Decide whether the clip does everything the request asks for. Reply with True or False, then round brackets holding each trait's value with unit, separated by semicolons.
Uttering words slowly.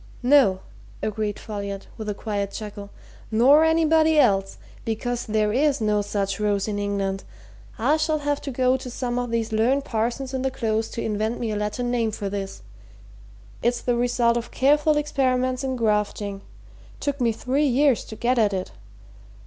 False (170 wpm)